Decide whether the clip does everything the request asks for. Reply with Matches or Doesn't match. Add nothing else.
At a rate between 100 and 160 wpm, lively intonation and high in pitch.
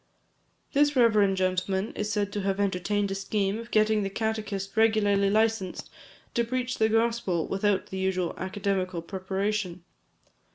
Doesn't match